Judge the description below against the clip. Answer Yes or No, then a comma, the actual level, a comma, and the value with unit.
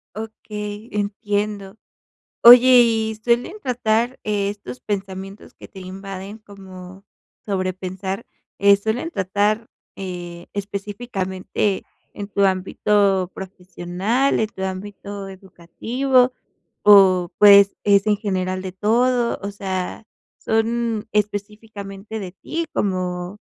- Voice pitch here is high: Yes, high, 200 Hz